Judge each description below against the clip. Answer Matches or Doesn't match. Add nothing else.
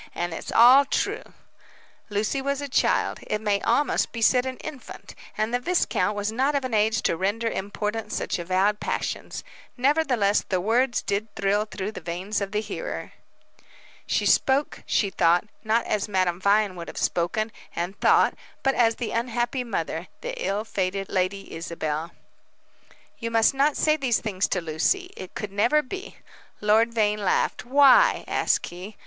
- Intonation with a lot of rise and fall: Doesn't match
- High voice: Matches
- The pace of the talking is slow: Doesn't match